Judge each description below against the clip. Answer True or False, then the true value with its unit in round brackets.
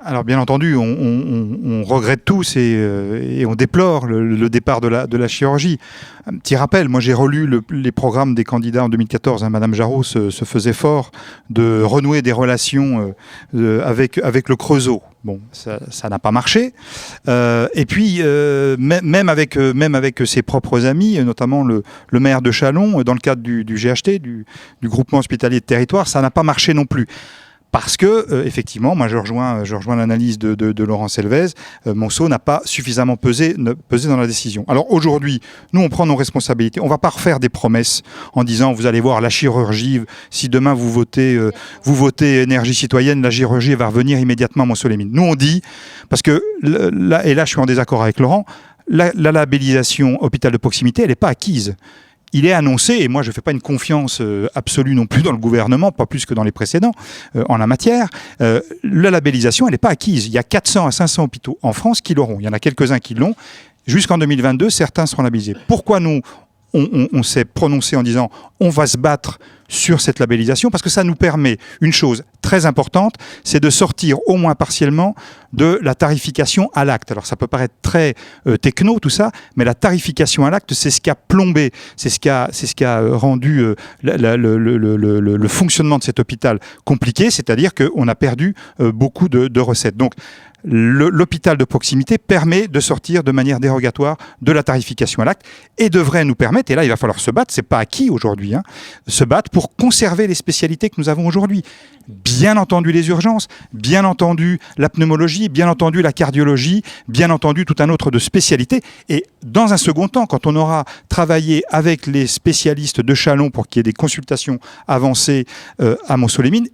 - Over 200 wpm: True (210 wpm)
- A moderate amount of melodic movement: True (4.9 semitones)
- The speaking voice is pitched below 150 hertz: True (135 Hz)